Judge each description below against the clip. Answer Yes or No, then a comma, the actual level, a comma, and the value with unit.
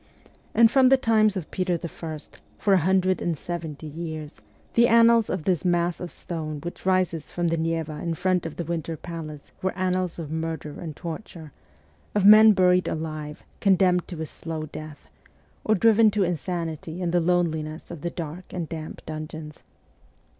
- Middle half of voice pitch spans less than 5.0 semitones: Yes, average, 2.8 semitones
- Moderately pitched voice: Yes, medium, 170 Hz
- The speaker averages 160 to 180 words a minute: Yes, average, 175 wpm